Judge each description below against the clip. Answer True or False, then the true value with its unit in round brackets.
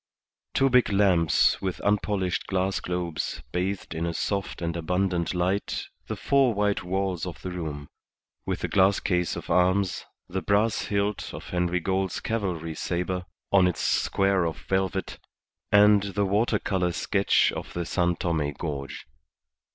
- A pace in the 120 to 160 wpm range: True (150 wpm)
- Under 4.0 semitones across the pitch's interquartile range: True (2.4 semitones)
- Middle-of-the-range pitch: False (95 Hz)